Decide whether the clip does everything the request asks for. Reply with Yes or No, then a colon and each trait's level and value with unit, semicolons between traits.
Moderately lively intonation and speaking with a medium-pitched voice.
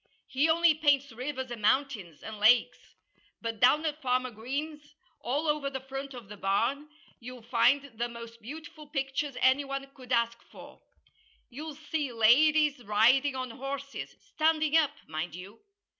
No: average, 4.0 semitones; very high, 265 Hz